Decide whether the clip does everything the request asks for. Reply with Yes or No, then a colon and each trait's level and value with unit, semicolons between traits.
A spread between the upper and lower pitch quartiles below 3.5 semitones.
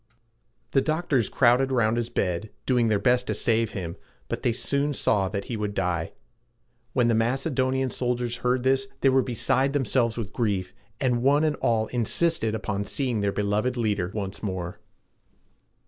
No: average, 4.0 semitones